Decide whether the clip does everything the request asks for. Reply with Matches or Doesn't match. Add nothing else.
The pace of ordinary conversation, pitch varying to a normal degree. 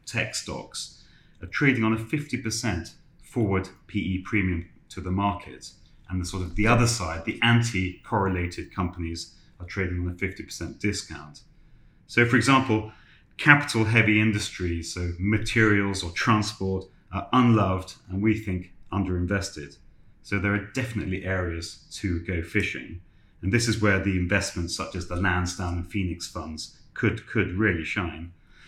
Matches